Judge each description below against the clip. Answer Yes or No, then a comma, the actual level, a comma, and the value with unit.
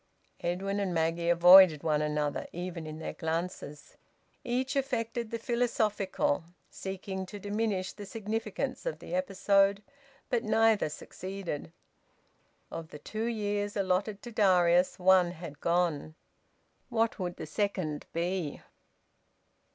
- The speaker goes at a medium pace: No, slow, 120 wpm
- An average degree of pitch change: Yes, average, 4.1 semitones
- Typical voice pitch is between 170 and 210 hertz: Yes, high, 190 Hz